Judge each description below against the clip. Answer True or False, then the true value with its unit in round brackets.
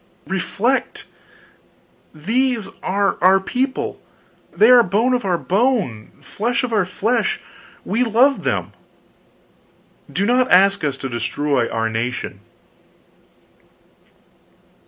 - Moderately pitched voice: False (200 Hz)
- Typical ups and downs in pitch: False (6.1 semitones)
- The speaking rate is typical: False (110 wpm)